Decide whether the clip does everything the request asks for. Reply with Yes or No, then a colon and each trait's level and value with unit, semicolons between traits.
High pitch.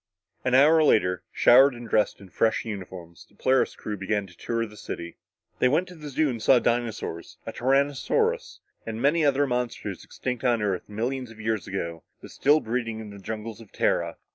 No: low, 115 Hz